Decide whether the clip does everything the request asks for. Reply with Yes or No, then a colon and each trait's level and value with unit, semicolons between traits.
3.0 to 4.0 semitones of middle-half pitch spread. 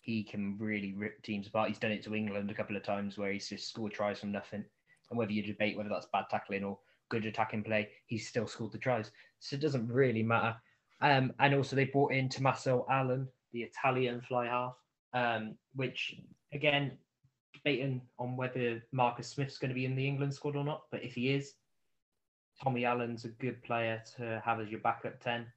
Yes: average, 3.3 semitones